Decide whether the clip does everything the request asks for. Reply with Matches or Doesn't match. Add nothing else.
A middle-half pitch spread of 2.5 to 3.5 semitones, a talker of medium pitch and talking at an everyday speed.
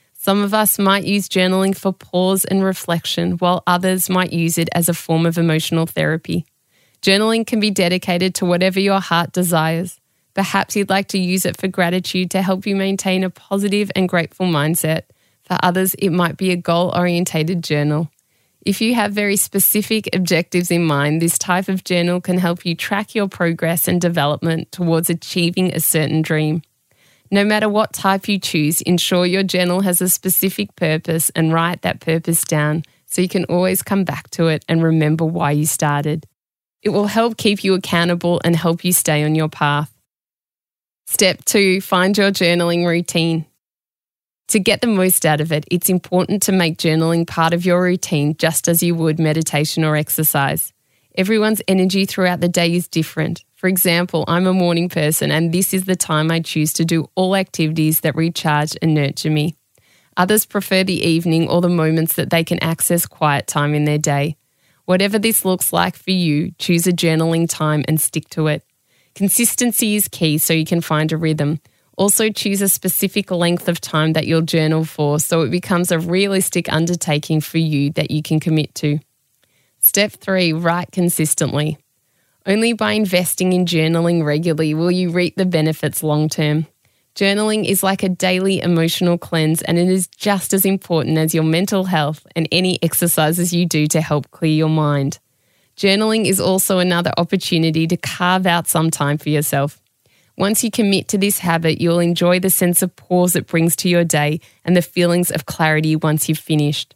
Matches